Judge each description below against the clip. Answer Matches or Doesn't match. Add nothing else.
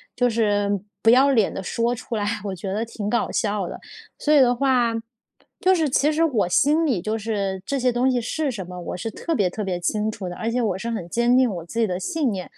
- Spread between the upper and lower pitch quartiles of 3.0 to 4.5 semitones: Matches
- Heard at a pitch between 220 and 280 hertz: Matches